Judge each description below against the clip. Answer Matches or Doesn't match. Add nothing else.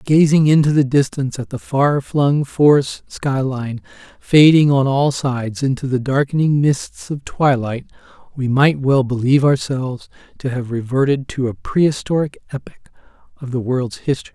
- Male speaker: Matches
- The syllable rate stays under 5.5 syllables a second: Matches